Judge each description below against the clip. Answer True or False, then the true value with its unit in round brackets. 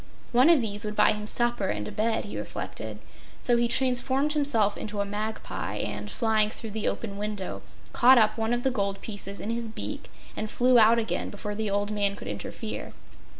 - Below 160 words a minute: False (200 wpm)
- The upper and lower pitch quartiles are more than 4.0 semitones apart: False (2.5 semitones)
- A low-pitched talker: False (220 Hz)